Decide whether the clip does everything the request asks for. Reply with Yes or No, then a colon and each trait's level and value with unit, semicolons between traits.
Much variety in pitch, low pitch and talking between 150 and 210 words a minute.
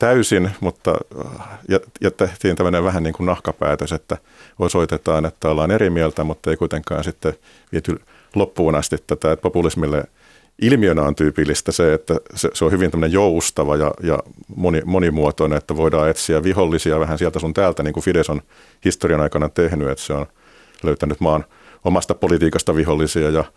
No: narrow, 2.5 semitones; very low, 80 Hz; fast, 155 wpm